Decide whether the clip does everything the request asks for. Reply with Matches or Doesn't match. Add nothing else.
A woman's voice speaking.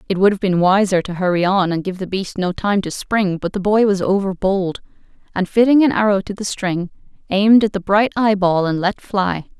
Matches